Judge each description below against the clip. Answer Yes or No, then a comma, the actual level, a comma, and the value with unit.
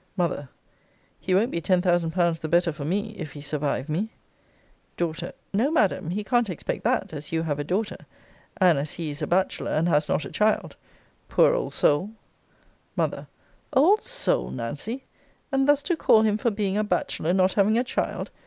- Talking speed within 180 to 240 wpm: Yes, average, 190 wpm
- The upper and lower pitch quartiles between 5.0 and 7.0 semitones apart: Yes, wide, 5.6 semitones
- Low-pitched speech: No, medium, 185 Hz